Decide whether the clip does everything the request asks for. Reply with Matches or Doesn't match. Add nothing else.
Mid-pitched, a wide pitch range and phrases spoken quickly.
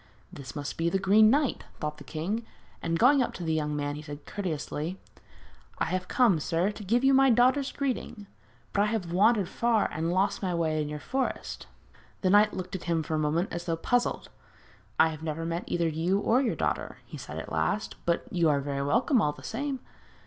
Matches